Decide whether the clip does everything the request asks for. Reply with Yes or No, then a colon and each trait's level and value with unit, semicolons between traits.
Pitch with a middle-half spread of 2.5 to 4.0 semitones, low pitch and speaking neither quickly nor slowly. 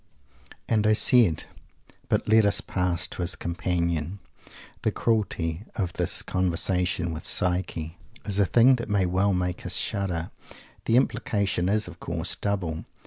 Yes: average, 2.9 semitones; very low, 90 Hz; average, 145 wpm